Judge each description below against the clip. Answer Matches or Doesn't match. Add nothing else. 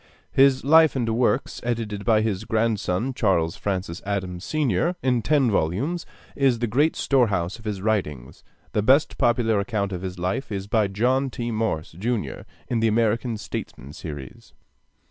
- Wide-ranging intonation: Doesn't match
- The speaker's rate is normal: Matches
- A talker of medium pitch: Doesn't match